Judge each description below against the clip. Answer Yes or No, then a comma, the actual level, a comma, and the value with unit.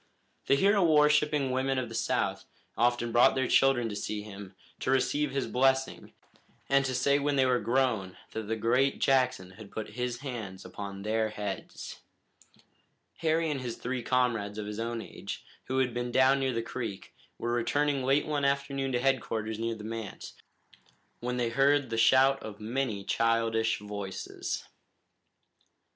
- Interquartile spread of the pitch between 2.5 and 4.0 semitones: Yes, average, 3.3 semitones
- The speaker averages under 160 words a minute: No, average, 165 wpm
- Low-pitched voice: Yes, low, 125 Hz